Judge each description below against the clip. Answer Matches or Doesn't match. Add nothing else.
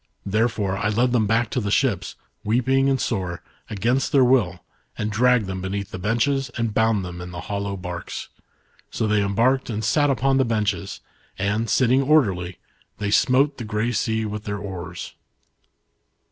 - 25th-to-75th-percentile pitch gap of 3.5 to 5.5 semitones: Matches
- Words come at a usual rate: Matches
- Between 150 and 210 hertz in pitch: Doesn't match